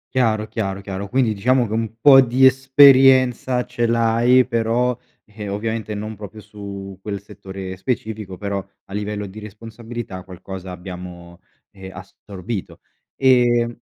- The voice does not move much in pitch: No, average, 3.5 semitones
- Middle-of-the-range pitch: No, low, 110 Hz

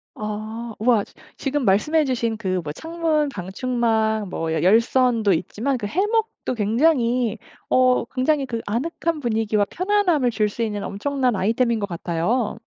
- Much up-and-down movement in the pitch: No, average, 4.6 semitones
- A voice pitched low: No, high, 235 Hz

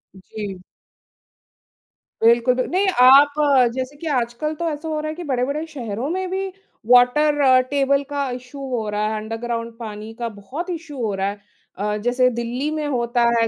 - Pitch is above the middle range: Yes, very high, 255 Hz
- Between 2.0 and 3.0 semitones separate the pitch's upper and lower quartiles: No, average, 4.4 semitones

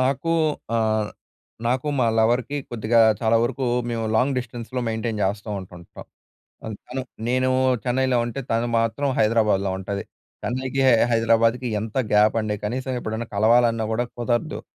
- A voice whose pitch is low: Yes, low, 115 Hz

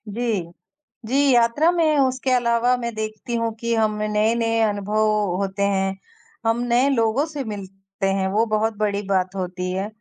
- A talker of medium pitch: No, high, 215 Hz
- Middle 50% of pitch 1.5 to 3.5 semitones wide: Yes, average, 3.1 semitones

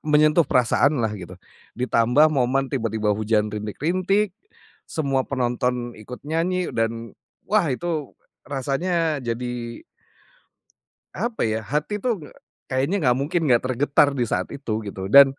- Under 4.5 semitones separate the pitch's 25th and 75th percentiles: No, average, 4.9 semitones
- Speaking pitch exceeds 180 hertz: No, low, 135 Hz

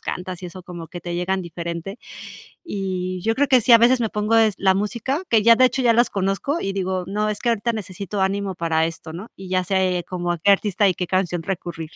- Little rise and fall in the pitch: No, average, 3.2 semitones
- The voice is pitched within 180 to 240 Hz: Yes, high, 190 Hz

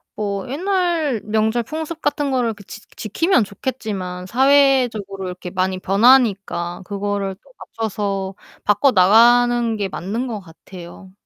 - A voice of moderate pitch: No, high, 215 Hz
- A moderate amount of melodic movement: Yes, average, 4.7 semitones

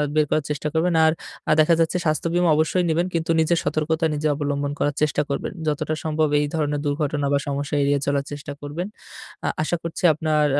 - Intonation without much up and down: Yes, narrow, 1.8 semitones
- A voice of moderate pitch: Yes, medium, 155 Hz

